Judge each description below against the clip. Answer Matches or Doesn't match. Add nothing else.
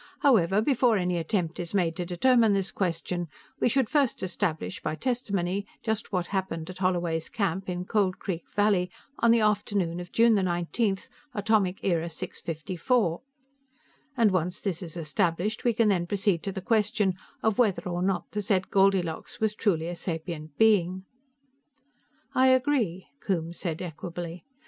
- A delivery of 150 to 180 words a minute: Matches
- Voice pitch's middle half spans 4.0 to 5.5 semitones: Doesn't match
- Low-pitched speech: Doesn't match